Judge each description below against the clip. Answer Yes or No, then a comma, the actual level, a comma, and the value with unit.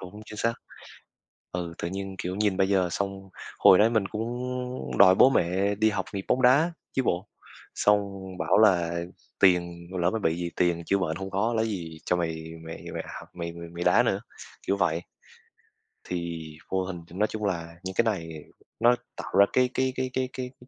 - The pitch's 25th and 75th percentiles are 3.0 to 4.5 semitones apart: Yes, average, 3.8 semitones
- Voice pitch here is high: No, very low, 95 Hz